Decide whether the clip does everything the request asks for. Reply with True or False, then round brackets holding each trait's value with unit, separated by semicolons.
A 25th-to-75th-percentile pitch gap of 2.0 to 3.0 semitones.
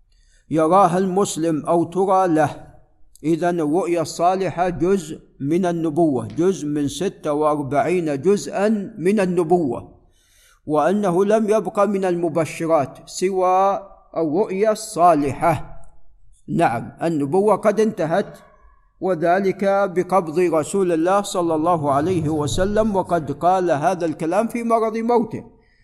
False (3.5 semitones)